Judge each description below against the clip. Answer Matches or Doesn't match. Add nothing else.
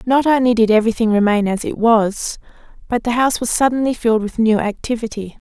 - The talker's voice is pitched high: Matches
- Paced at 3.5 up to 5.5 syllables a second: Doesn't match